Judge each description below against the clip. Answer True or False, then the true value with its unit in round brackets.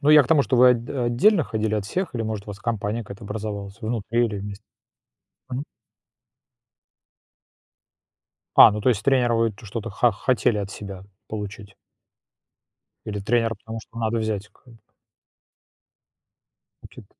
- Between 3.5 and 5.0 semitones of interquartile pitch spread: False (2.8 semitones)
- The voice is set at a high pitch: False (110 Hz)